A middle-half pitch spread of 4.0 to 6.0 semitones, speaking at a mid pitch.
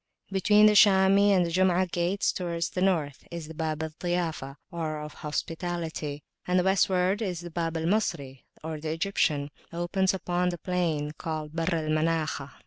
No: average, 2.9 semitones; medium, 170 Hz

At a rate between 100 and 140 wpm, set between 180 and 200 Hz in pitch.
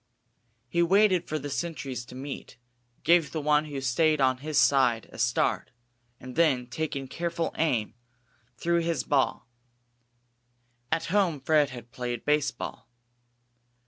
No: slow, 135 wpm; medium, 145 Hz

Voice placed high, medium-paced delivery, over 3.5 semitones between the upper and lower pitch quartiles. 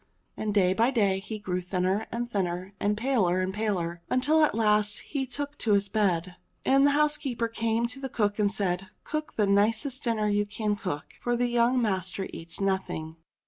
Yes: high, 210 Hz; average, 185 wpm; average, 4.0 semitones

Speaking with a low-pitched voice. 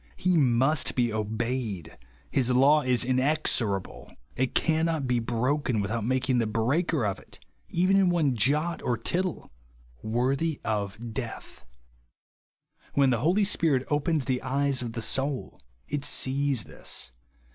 Yes: low, 130 Hz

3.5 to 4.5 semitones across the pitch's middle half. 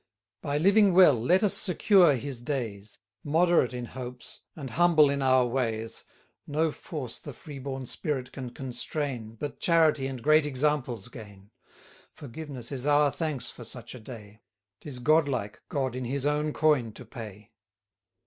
Yes: average, 3.9 semitones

